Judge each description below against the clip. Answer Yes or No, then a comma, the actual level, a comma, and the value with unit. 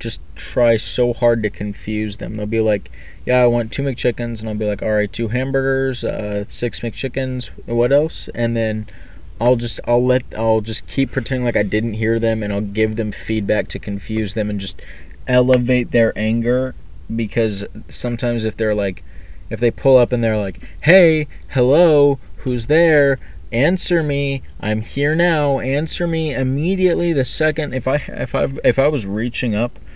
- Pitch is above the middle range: No, low, 120 Hz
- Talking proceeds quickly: No, average, 180 wpm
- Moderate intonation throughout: Yes, average, 3.7 semitones